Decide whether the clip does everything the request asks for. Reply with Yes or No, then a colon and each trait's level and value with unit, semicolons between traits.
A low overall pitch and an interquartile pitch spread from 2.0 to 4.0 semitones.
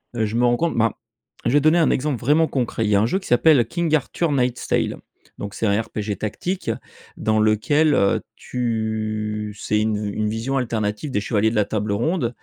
No: low, 115 Hz; average, 4.7 semitones